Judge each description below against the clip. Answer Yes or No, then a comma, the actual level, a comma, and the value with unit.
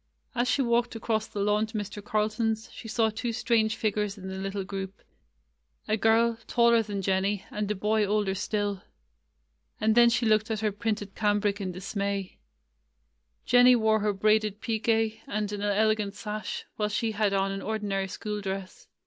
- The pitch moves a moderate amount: No, narrow, 1.7 semitones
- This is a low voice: No, high, 210 Hz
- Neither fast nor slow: Yes, average, 180 wpm